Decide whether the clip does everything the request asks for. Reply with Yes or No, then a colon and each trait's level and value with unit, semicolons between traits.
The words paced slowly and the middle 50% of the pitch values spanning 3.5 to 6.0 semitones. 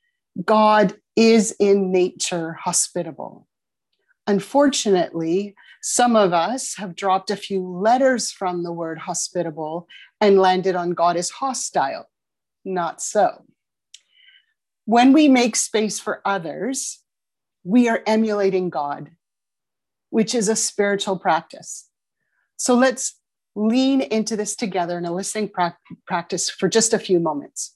Yes: slow, 125 wpm; average, 4.4 semitones